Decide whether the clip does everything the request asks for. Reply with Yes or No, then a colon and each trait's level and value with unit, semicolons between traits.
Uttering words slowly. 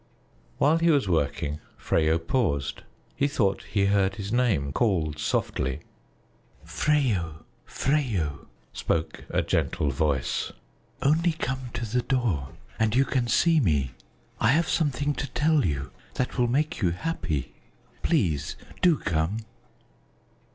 Yes: slow, 130 wpm